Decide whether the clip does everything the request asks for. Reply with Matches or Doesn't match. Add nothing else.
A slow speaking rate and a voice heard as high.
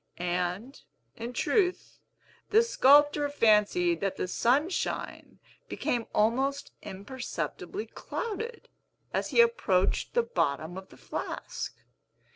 Matches